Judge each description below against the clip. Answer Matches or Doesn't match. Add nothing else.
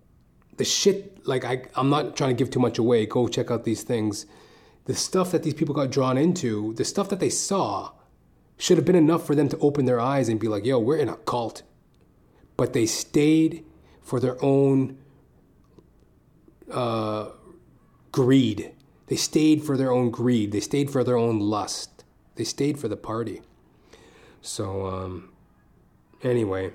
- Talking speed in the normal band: Matches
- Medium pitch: Doesn't match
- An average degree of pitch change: Matches